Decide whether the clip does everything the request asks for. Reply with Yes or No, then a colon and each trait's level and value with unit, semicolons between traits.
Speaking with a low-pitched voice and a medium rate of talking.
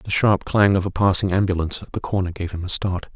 No: very low, 95 Hz; fast, 265 wpm